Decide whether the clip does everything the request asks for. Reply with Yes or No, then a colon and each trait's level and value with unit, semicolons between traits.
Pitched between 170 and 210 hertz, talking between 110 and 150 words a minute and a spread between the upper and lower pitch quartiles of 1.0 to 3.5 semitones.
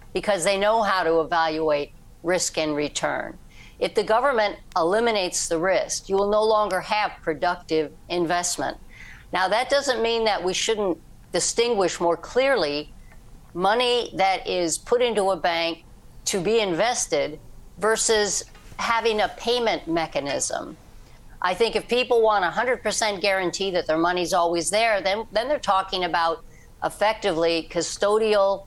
No: high, 190 Hz; average, 140 wpm; average, 4.7 semitones